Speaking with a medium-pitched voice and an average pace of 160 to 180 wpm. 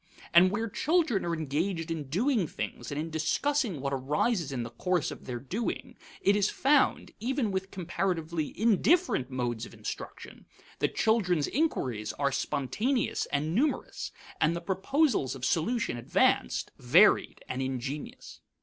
No: medium, 170 Hz; average, 145 wpm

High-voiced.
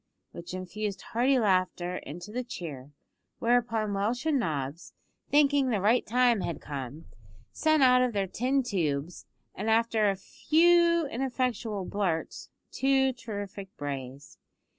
Yes: high, 215 Hz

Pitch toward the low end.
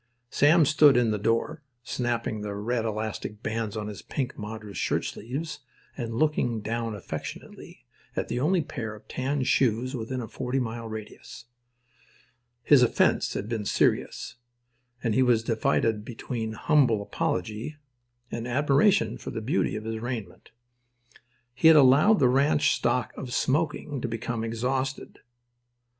Yes: low, 120 Hz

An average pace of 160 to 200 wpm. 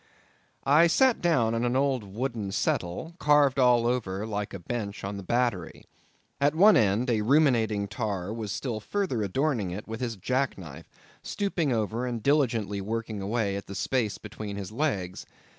Yes: average, 170 wpm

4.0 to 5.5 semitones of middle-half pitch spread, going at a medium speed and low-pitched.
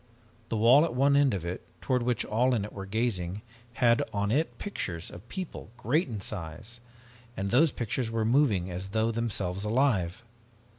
Yes: average, 4.4 semitones; average, 180 wpm; low, 115 Hz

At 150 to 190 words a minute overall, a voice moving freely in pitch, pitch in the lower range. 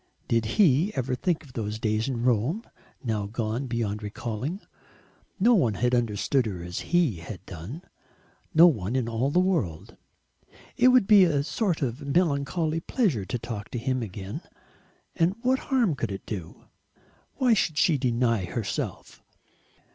Yes: average, 155 wpm; wide, 7.4 semitones; low, 125 Hz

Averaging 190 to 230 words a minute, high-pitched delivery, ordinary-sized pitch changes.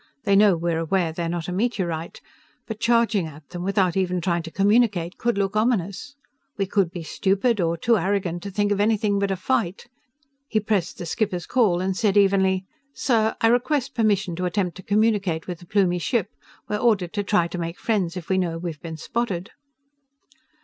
Yes: average, 195 wpm; high, 195 Hz; average, 3.6 semitones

